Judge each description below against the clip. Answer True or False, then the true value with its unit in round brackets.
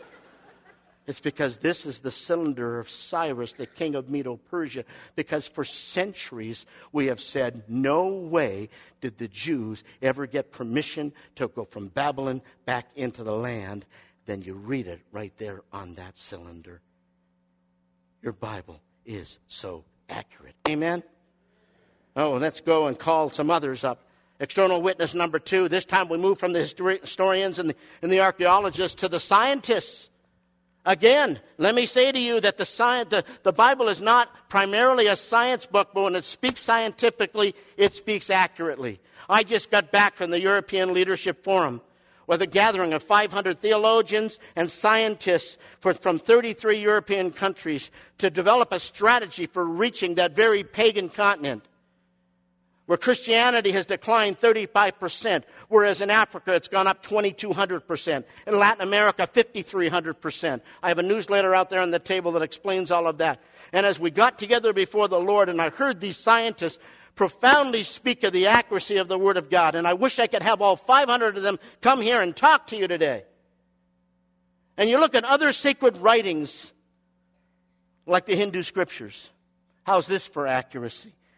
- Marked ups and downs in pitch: True (6.2 semitones)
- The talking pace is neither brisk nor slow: True (160 wpm)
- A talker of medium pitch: True (180 Hz)